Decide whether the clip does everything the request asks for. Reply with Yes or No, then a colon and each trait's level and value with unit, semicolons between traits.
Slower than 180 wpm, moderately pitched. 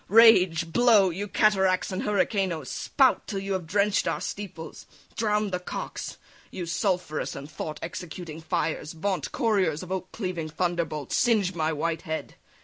Yes: average, 145 wpm; medium, 180 Hz